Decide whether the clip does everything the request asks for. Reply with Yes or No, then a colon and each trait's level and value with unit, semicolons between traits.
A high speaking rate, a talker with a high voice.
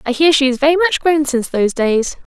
Yes: fast, 260 wpm; very high, 285 Hz